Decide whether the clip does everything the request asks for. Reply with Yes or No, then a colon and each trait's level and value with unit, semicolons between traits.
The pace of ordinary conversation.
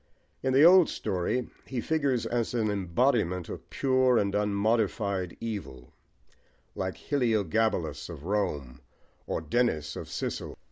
No: slow, 125 wpm